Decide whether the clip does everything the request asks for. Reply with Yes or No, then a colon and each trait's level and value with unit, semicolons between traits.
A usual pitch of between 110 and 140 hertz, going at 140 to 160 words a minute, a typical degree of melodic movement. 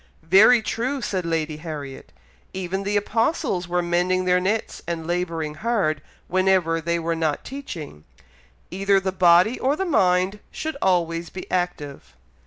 No: medium, 180 Hz; average, 145 wpm; average, 3.1 semitones